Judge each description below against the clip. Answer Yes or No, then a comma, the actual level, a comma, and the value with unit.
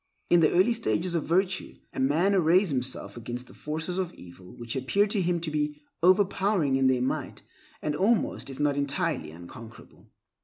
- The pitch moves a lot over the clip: Yes, wide, 5.9 semitones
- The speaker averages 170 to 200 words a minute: Yes, average, 180 wpm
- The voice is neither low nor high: Yes, medium, 155 Hz